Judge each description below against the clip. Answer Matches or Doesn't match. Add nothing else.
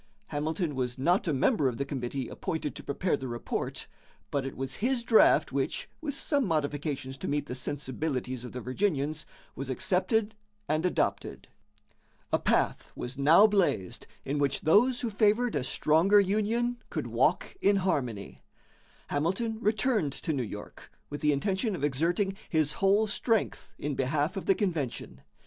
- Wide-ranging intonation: Matches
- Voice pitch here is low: Doesn't match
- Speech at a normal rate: Matches